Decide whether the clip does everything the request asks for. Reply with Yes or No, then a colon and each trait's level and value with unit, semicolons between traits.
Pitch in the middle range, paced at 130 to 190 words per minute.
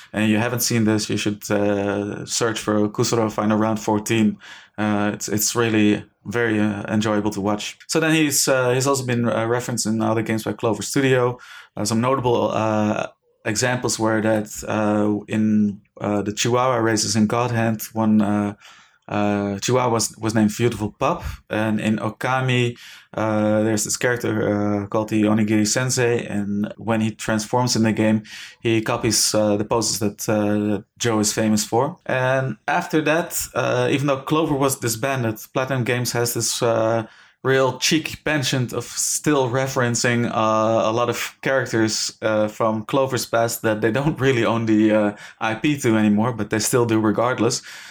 No: low, 110 Hz; average, 170 wpm